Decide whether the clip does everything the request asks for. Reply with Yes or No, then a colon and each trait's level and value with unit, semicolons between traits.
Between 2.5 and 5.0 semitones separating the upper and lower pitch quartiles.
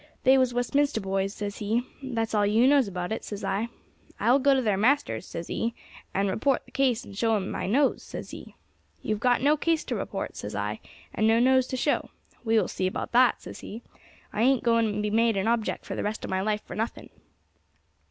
Yes: average, 3.8 semitones